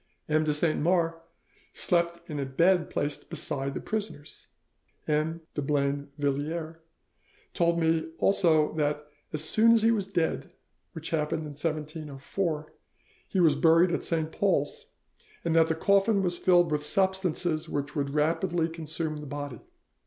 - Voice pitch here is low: No, medium, 160 Hz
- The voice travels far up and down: No, narrow, 2.5 semitones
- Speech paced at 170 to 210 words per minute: No, average, 145 wpm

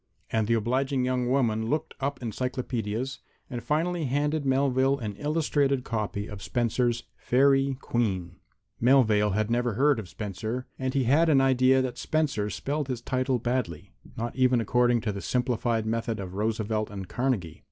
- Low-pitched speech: Yes, low, 125 Hz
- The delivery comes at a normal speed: Yes, average, 160 wpm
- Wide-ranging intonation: No, average, 3.4 semitones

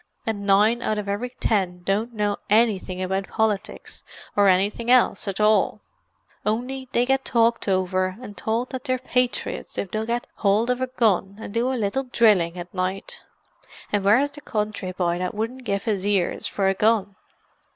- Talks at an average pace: Yes, average, 175 wpm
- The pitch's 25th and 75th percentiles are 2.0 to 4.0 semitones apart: Yes, average, 3.5 semitones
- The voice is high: Yes, high, 210 Hz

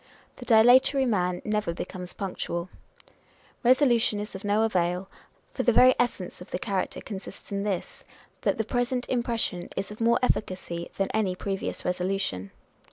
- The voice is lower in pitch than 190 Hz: No, high, 205 Hz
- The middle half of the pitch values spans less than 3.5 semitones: No, average, 4.5 semitones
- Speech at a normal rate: Yes, average, 155 wpm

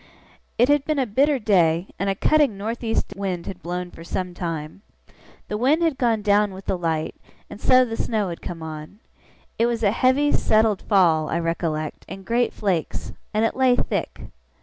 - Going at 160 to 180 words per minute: No, average, 195 wpm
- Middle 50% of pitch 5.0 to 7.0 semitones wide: Yes, wide, 5.4 semitones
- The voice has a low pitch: No, high, 205 Hz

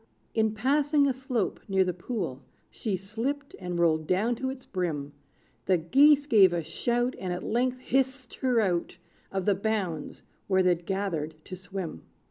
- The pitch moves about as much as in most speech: No, wide, 6.1 semitones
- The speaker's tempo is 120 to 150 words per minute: No, average, 165 wpm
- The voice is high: Yes, high, 200 Hz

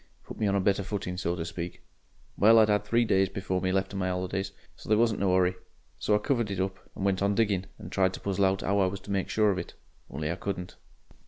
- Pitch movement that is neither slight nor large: No, narrow, 1.7 semitones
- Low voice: Yes, very low, 95 Hz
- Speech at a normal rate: No, fast, 265 wpm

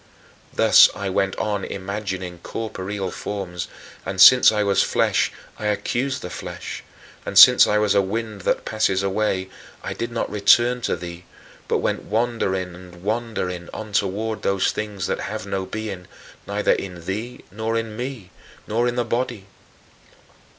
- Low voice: Yes, low, 100 Hz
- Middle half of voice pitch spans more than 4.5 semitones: No, average, 2.8 semitones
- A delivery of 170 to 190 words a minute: No, average, 155 wpm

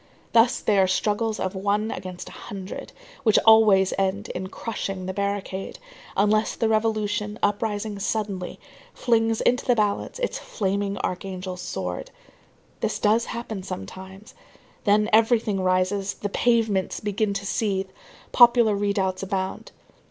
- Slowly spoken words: Yes, slow, 130 wpm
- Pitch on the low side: No, high, 205 Hz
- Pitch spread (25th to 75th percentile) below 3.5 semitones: Yes, narrow, 2.4 semitones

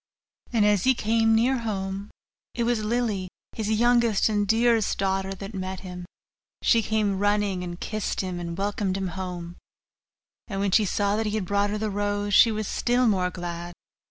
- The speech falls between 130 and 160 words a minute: No, average, 185 wpm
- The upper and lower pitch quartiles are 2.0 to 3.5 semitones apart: Yes, narrow, 2.6 semitones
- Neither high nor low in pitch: No, high, 205 Hz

